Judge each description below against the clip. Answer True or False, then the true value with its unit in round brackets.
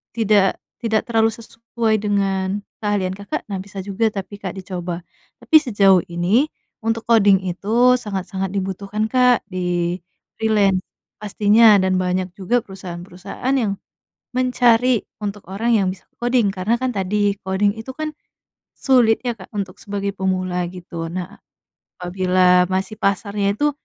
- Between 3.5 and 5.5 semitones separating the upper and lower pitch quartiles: False (3.1 semitones)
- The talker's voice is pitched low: False (200 Hz)